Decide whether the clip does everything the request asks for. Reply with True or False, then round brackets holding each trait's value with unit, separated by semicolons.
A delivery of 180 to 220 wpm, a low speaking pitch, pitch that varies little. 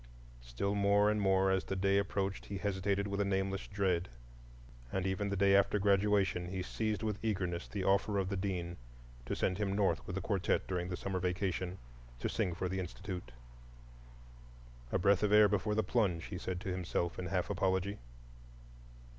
True (185 wpm; 95 Hz; 1.6 semitones)